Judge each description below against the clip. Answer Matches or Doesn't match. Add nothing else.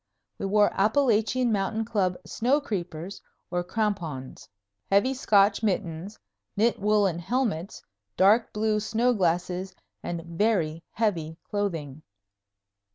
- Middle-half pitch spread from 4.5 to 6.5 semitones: Doesn't match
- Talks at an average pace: Doesn't match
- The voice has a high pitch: Matches